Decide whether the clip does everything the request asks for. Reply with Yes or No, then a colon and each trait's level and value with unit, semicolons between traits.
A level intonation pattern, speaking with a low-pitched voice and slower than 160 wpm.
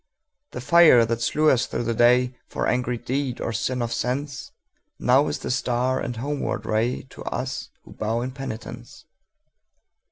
Yes: narrow, 1.9 semitones; low, 125 Hz; average, 150 wpm